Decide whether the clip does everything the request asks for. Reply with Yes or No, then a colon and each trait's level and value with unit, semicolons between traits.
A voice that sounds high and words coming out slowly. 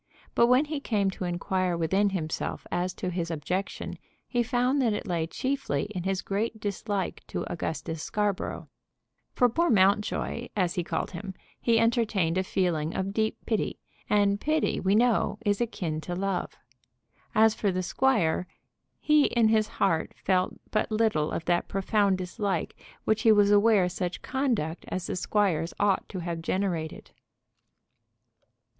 No: high, 195 Hz; average, 155 wpm